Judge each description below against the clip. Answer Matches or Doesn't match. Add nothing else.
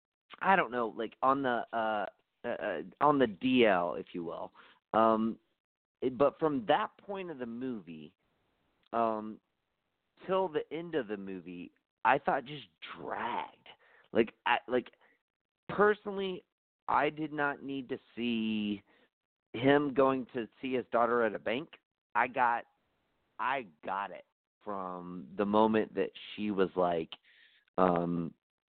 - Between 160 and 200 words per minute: Doesn't match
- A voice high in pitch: Doesn't match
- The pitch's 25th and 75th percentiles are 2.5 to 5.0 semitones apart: Doesn't match